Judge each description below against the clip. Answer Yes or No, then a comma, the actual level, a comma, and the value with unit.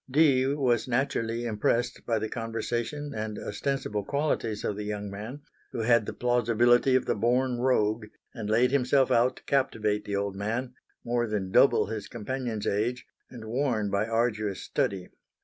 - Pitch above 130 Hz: No, low, 115 Hz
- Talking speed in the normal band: Yes, average, 165 wpm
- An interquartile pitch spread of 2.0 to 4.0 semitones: Yes, average, 3.0 semitones